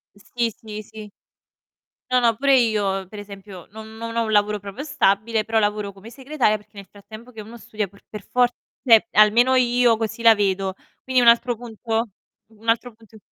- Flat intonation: Yes, narrow, 2.3 semitones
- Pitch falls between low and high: No, high, 220 Hz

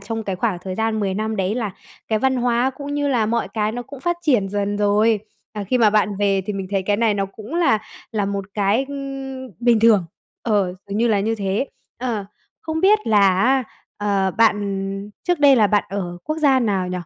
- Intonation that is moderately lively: Yes, average, 4.0 semitones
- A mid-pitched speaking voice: No, high, 215 Hz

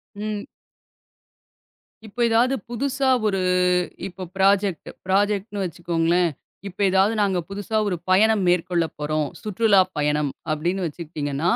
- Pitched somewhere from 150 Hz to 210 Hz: Yes, high, 190 Hz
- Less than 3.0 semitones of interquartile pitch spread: No, average, 3.6 semitones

